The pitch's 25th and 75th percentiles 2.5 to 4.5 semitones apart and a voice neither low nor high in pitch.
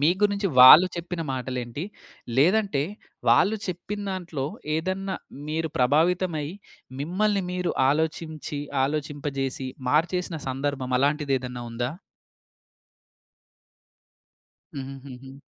No: average, 5.1 semitones; medium, 150 Hz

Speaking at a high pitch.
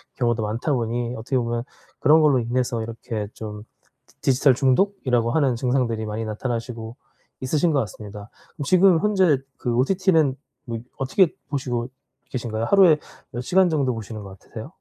No: low, 125 Hz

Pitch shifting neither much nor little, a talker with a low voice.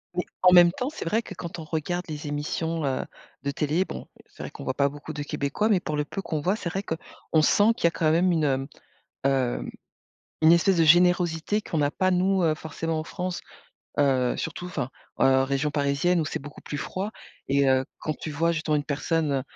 No: average, 3.6 semitones; medium, 160 Hz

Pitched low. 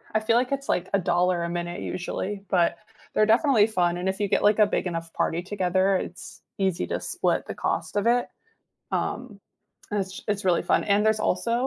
No: high, 190 Hz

